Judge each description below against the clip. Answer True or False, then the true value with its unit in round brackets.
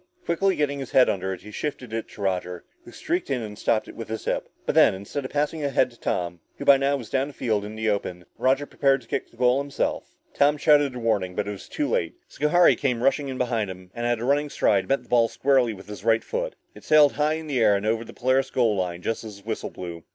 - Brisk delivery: True (270 wpm)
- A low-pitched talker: True (120 Hz)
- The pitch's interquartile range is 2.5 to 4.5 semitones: False (5.2 semitones)